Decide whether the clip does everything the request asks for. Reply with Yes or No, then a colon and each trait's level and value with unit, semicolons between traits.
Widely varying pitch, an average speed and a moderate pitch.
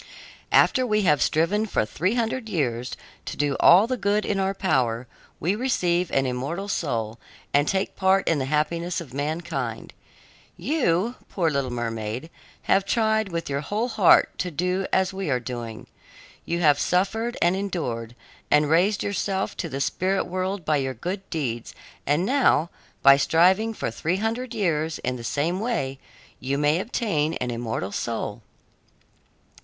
Yes: wide, 6.2 semitones; average, 160 wpm; medium, 170 Hz